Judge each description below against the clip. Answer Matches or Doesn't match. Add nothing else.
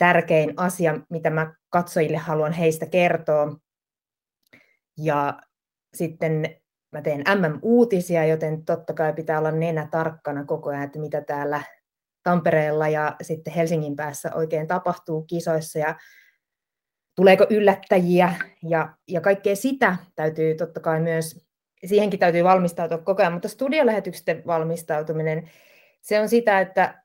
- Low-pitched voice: Doesn't match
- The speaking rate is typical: Matches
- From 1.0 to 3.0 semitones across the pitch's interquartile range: Matches